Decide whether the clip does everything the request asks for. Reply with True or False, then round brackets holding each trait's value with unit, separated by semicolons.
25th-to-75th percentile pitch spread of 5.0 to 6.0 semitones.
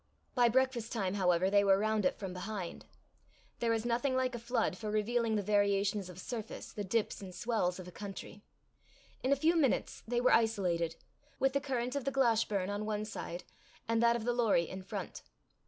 False (3.6 semitones)